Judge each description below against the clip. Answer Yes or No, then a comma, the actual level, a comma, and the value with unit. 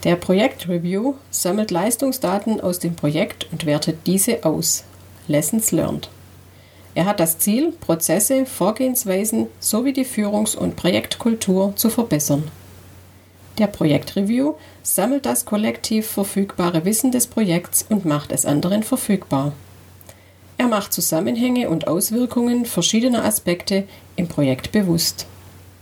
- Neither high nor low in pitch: Yes, medium, 180 Hz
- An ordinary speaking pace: No, slow, 120 wpm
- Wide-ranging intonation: Yes, wide, 6.9 semitones